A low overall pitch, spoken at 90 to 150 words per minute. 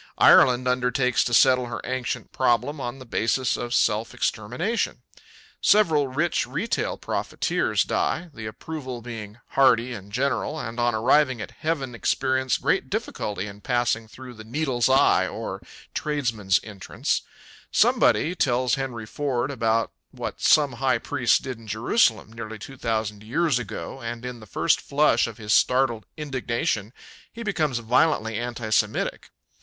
Yes: low, 125 Hz; average, 145 wpm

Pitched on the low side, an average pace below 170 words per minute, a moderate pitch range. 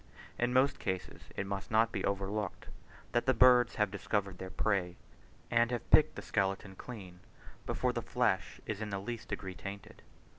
No: low, 100 Hz; average, 175 wpm; average, 3.3 semitones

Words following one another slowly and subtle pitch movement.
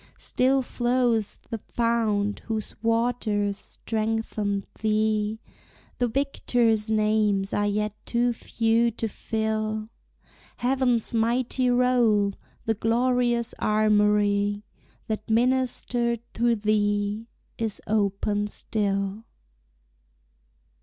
Yes: slow, 85 wpm; narrow, 2.2 semitones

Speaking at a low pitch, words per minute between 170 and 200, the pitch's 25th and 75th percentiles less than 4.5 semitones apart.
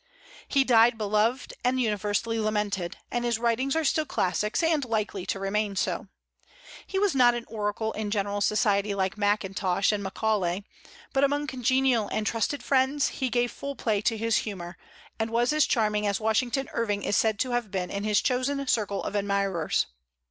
No: high, 220 Hz; average, 175 wpm; average, 3.5 semitones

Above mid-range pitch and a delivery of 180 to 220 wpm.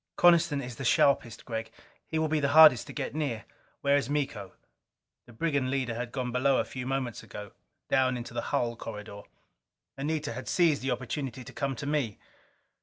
No: low, 130 Hz; average, 185 wpm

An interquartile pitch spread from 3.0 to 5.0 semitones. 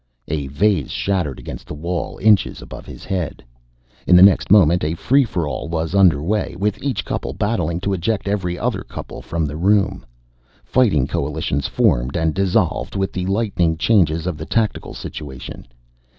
Yes: average, 4.3 semitones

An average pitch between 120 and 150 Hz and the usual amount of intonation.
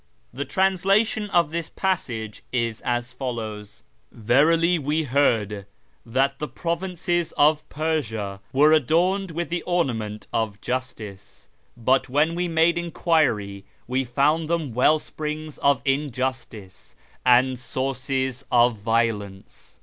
No: low, 135 Hz; wide, 5.9 semitones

